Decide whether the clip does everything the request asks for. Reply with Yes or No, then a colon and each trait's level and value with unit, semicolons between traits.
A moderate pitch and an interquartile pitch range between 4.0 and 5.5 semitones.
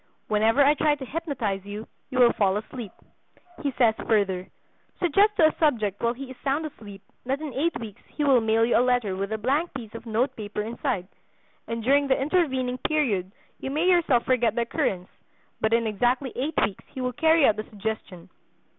No: high, 245 Hz; average, 4.6 semitones